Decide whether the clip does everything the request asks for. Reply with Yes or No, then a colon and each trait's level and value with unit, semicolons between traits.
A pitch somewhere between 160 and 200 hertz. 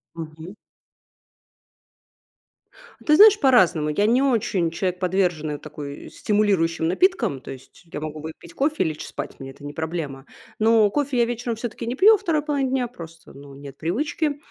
Yes: high, 190 Hz